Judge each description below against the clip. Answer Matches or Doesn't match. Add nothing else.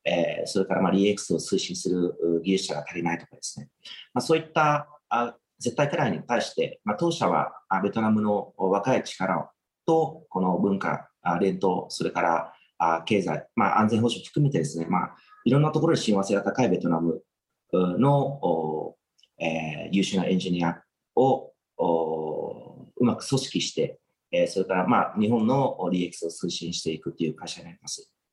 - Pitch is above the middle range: Doesn't match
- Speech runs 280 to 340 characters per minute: Matches